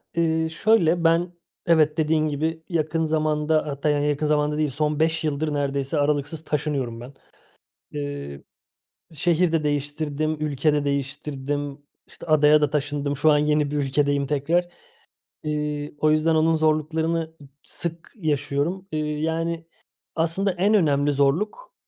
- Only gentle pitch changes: Yes, narrow, 1.9 semitones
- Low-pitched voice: No, medium, 150 Hz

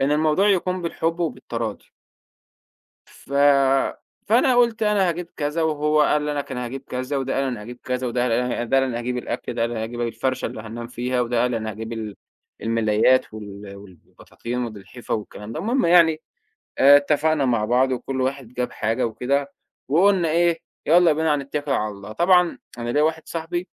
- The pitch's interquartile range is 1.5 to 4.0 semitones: No, average, 5.3 semitones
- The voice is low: Yes, low, 130 Hz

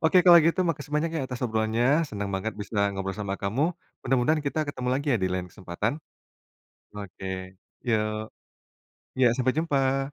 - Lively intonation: Yes, wide, 5.8 semitones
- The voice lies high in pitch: No, low, 120 Hz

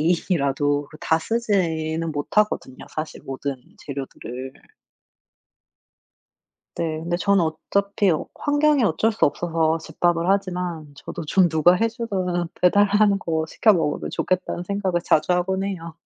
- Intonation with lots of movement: No, average, 4.0 semitones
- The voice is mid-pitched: Yes, medium, 175 Hz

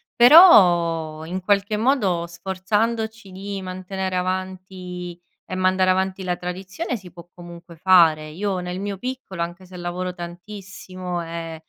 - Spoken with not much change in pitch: Yes, narrow, 1.9 semitones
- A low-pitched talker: No, medium, 185 Hz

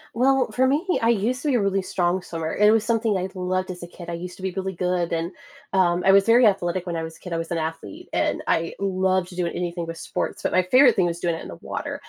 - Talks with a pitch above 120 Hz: Yes, medium, 185 Hz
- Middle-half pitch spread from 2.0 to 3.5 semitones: Yes, average, 3.1 semitones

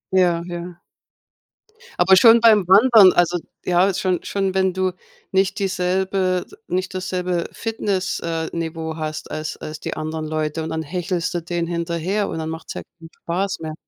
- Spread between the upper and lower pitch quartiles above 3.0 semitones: No, narrow, 2.5 semitones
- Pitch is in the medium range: Yes, medium, 180 Hz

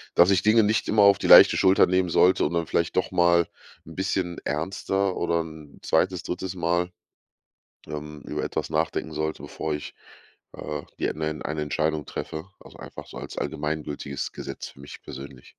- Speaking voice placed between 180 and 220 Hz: No, very low, 85 Hz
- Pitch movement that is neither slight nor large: Yes, average, 3.4 semitones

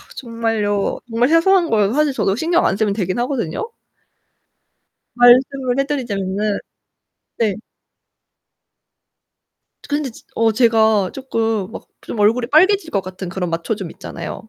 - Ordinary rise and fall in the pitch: Yes, average, 5.0 semitones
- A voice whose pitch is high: Yes, high, 225 Hz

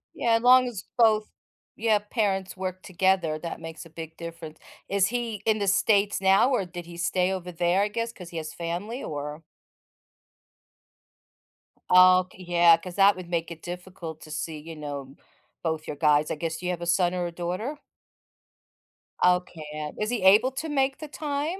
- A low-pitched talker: No, medium, 180 Hz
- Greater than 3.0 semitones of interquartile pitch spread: Yes, average, 4.0 semitones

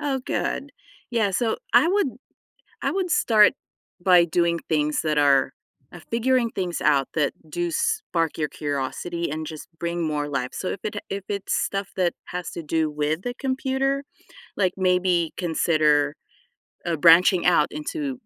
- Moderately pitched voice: Yes, medium, 175 Hz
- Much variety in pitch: Yes, wide, 5.7 semitones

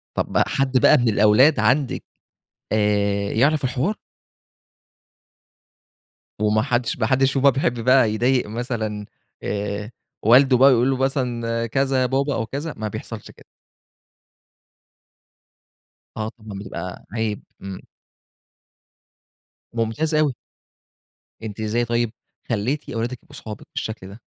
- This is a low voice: Yes, low, 120 Hz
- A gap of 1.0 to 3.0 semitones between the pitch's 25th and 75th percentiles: No, average, 3.7 semitones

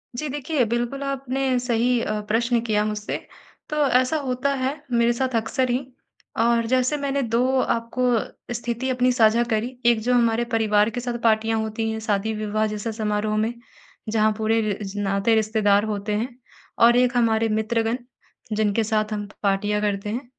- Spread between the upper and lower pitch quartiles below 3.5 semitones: Yes, narrow, 2.5 semitones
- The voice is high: Yes, high, 230 Hz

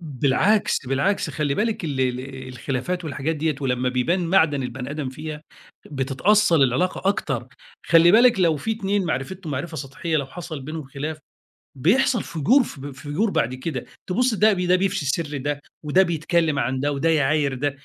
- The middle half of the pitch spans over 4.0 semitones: Yes, average, 5.1 semitones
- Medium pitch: Yes, medium, 155 Hz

